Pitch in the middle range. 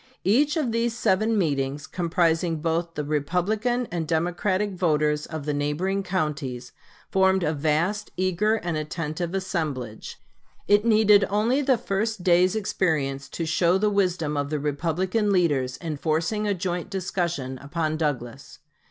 Yes: medium, 175 Hz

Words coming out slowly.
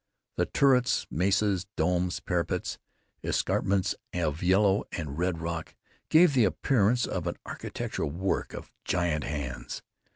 Yes: slow, 130 wpm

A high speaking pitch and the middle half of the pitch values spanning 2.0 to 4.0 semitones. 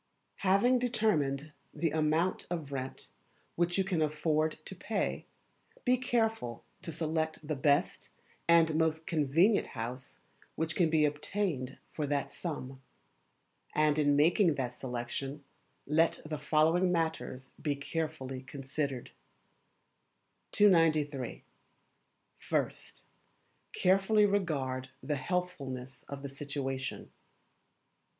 No: medium, 155 Hz; average, 3.7 semitones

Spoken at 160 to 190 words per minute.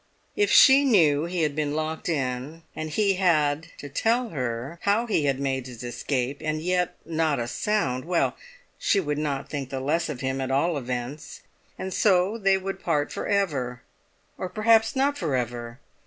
Yes: average, 180 wpm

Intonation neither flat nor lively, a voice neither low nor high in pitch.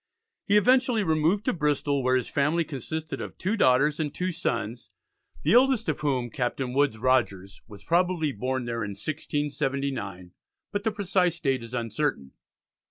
No: wide, 5.8 semitones; medium, 145 Hz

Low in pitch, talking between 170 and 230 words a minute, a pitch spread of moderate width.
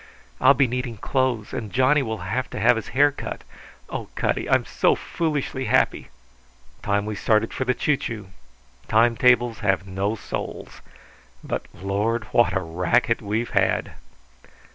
No: low, 115 Hz; average, 155 wpm; average, 3.8 semitones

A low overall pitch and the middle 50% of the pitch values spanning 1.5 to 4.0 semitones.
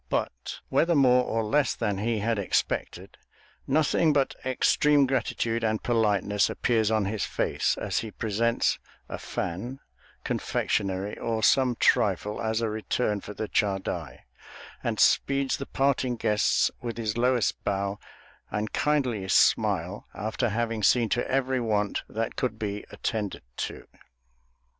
Yes: low, 115 Hz; average, 3.4 semitones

